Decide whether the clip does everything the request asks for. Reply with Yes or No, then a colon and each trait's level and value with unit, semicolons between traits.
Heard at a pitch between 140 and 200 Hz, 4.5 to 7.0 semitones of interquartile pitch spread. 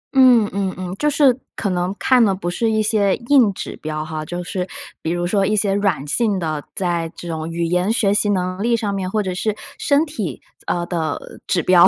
No: high, 190 Hz; average, 3.8 semitones